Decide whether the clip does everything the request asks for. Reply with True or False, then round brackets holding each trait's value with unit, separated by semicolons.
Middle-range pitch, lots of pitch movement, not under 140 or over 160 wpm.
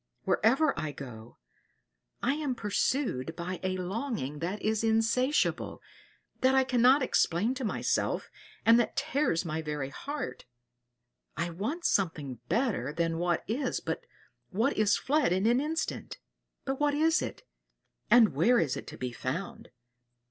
False (220 Hz; 7.9 semitones; 145 wpm)